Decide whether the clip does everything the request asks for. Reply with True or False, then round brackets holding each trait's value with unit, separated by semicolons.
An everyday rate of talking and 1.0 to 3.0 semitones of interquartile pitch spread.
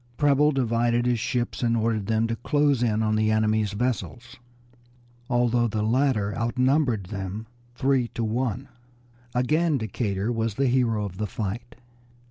True (145 wpm; 2.7 semitones)